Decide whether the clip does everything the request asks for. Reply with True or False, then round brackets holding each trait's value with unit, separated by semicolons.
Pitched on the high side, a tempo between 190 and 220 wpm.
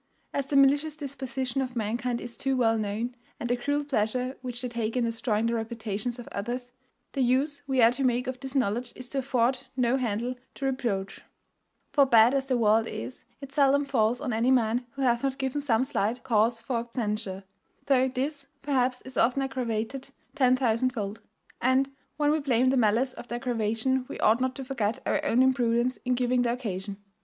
True (250 Hz; 200 wpm)